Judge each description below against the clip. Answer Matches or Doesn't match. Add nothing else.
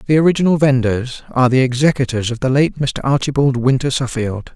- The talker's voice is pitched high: Doesn't match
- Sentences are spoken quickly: Doesn't match